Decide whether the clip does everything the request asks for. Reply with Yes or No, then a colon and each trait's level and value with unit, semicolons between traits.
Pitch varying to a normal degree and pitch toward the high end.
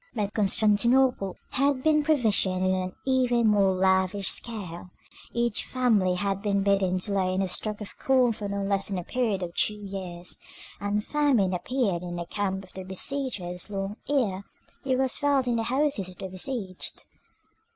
Yes: average, 4.6 semitones; high, 200 Hz